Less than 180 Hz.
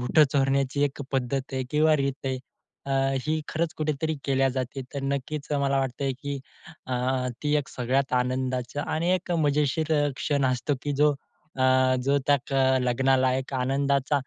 Yes: medium, 140 Hz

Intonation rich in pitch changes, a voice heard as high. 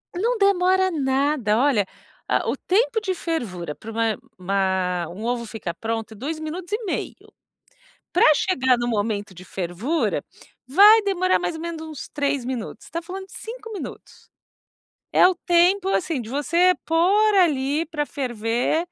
Yes: wide, 8.4 semitones; very high, 295 Hz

